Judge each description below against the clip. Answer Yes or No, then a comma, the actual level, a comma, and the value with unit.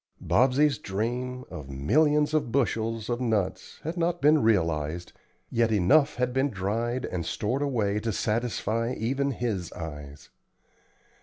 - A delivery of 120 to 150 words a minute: Yes, slow, 135 wpm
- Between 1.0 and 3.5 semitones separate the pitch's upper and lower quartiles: No, average, 5.0 semitones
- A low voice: Yes, low, 115 Hz